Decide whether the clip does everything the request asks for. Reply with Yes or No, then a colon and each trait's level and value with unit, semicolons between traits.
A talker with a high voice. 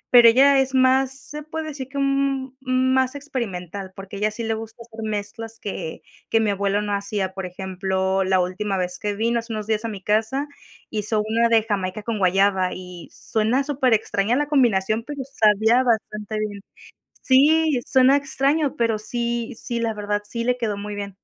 Yes: high, 225 Hz